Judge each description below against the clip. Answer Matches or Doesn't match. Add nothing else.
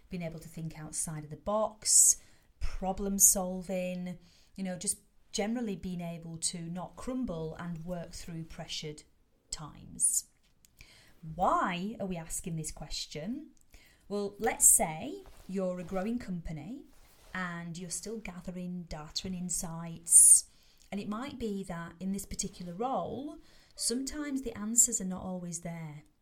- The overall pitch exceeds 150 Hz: Matches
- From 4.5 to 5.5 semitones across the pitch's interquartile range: Doesn't match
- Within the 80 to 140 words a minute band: Matches